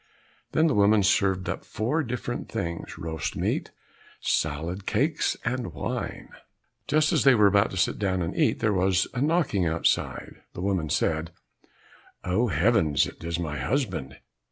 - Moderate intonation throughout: No, wide, 6.1 semitones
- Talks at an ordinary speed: Yes, average, 155 wpm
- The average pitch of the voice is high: No, very low, 95 Hz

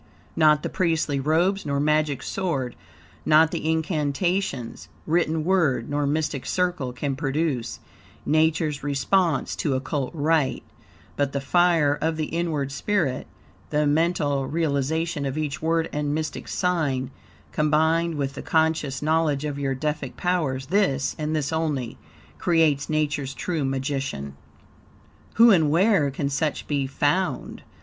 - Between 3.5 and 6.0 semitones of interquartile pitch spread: No, average, 2.7 semitones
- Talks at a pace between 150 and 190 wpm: No, slow, 135 wpm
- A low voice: No, medium, 150 Hz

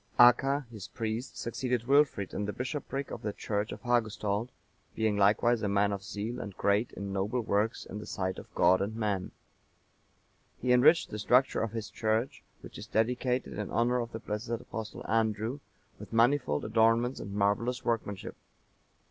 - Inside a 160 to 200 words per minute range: Yes, average, 170 wpm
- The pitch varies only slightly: No, average, 3.0 semitones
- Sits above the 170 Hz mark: No, low, 110 Hz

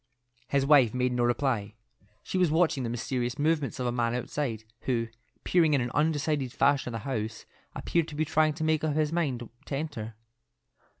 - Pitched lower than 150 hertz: Yes, low, 135 Hz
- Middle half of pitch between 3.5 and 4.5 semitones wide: Yes, average, 4.2 semitones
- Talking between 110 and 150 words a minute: No, average, 190 wpm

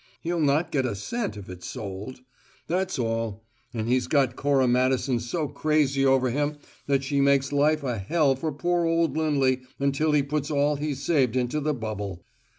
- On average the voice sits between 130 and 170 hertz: Yes, medium, 140 Hz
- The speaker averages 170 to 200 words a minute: Yes, average, 180 wpm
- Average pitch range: Yes, average, 3.4 semitones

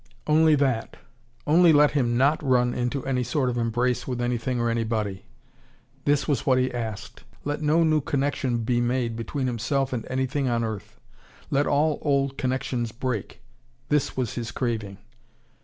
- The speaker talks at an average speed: Yes, average, 160 wpm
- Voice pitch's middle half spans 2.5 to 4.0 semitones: Yes, average, 3.1 semitones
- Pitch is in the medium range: No, low, 125 Hz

